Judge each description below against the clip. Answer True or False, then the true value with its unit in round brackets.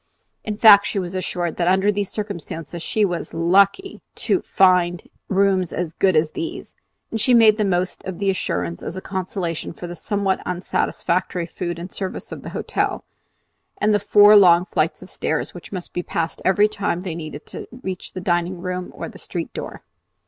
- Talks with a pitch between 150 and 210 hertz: True (185 Hz)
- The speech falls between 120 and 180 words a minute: False (190 wpm)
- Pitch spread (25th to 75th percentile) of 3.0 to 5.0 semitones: False (2.6 semitones)